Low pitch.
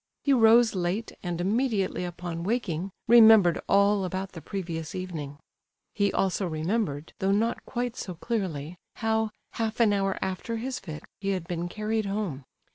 No: high, 195 Hz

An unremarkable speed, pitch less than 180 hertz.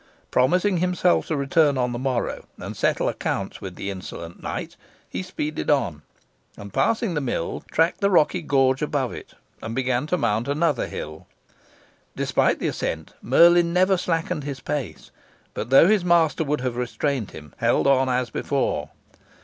Yes: average, 165 wpm; medium, 140 Hz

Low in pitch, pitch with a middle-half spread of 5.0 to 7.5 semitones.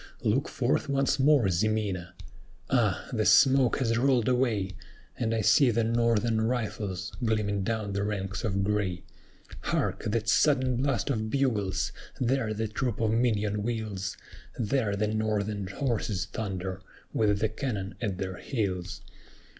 No: low, 110 Hz; average, 3.1 semitones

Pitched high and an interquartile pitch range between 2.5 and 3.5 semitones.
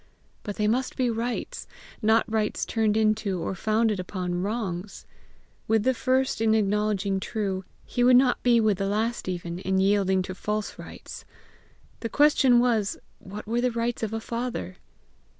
Yes: high, 215 Hz; average, 3.2 semitones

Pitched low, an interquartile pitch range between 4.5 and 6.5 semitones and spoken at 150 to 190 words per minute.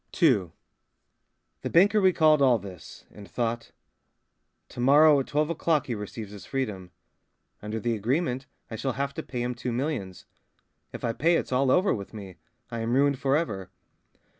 Yes: low, 125 Hz; average, 5.2 semitones; average, 170 wpm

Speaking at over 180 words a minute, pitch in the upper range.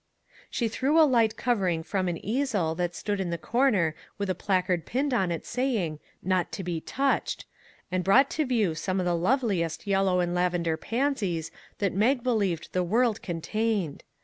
Yes: average, 195 wpm; high, 195 Hz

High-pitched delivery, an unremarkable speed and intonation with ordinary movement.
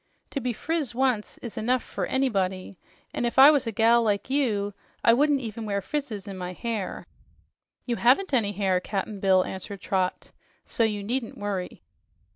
Yes: high, 220 Hz; average, 175 wpm; average, 4.2 semitones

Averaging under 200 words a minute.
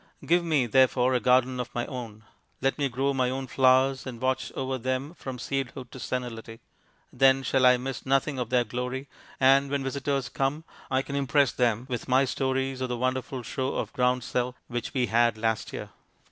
Yes: average, 190 wpm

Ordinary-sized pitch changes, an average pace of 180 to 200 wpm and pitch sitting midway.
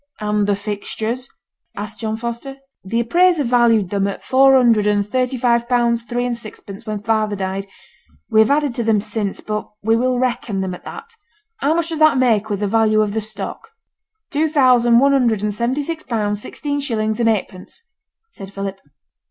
No: average, 3.4 semitones; average, 190 wpm; high, 230 Hz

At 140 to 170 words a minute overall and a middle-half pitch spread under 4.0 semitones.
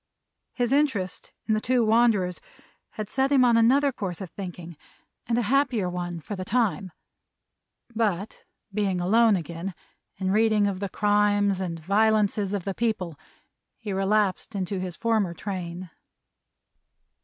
Yes: average, 145 wpm; average, 3.5 semitones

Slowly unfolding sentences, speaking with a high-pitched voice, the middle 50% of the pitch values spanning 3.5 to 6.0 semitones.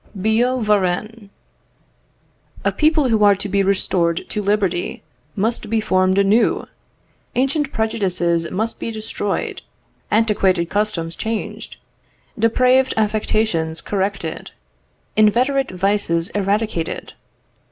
No: slow, 100 wpm; high, 210 Hz; average, 3.1 semitones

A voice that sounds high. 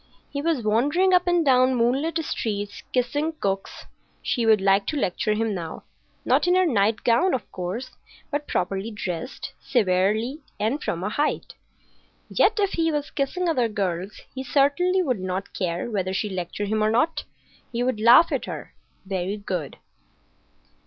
Yes: high, 230 Hz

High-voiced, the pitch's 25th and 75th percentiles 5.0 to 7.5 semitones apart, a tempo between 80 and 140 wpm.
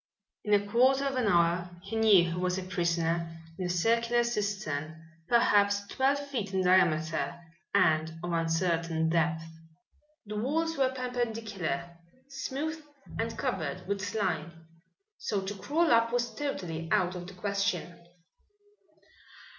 Yes: high, 195 Hz; wide, 5.6 semitones; slow, 135 wpm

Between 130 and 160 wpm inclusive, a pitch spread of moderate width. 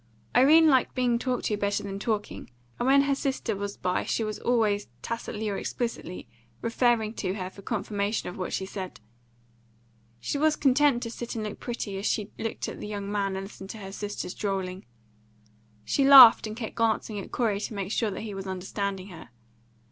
No: average, 195 wpm; average, 3.3 semitones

